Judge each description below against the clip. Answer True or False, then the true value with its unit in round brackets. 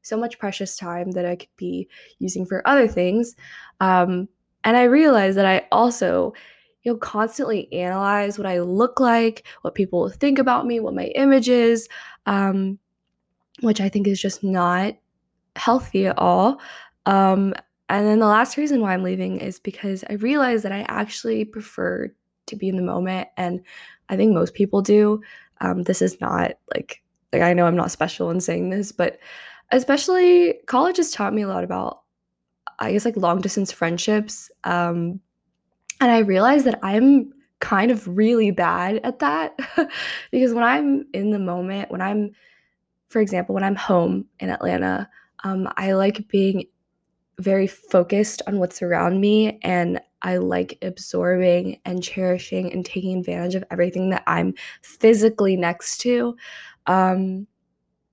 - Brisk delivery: False (160 wpm)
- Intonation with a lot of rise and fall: False (4.2 semitones)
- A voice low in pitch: False (200 Hz)